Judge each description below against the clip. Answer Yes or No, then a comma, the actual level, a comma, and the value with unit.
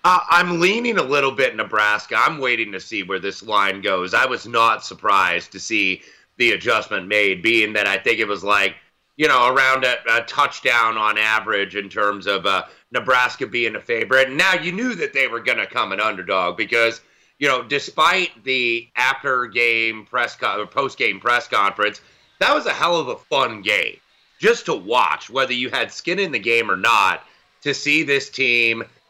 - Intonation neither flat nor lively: No, wide, 8.4 semitones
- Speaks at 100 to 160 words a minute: No, average, 200 wpm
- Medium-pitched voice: No, low, 120 Hz